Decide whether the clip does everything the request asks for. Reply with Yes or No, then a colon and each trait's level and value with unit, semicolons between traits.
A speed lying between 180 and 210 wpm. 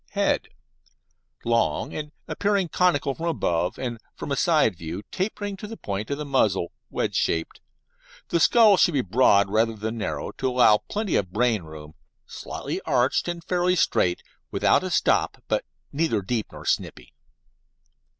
No: average, 160 wpm